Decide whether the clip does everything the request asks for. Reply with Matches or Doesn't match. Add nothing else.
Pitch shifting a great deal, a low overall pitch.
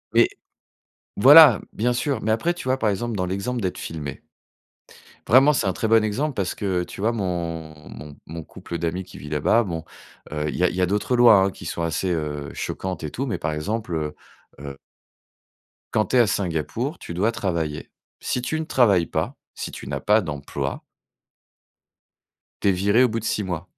Matches